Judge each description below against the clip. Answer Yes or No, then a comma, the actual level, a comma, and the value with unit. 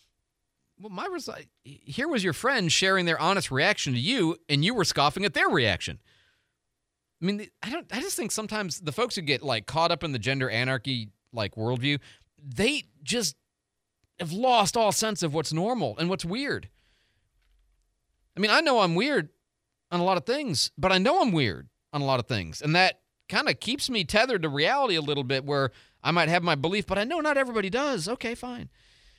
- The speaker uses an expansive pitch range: Yes, wide, 7.4 semitones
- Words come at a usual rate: No, fast, 210 wpm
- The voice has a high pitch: No, medium, 170 Hz